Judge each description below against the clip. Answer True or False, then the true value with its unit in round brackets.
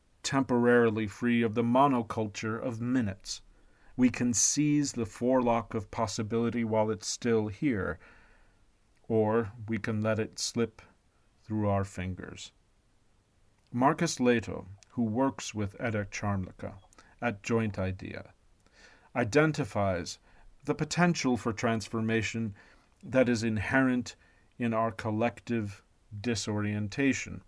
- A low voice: True (110 Hz)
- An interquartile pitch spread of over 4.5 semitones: False (3.0 semitones)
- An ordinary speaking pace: False (105 wpm)